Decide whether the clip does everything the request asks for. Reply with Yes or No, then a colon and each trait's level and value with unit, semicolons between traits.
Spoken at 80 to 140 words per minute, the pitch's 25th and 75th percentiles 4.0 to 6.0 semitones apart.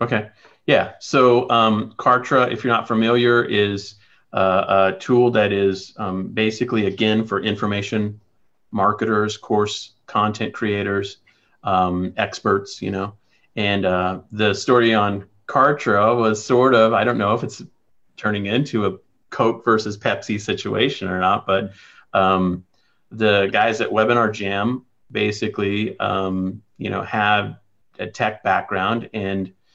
No: slow, 135 wpm; narrow, 2.4 semitones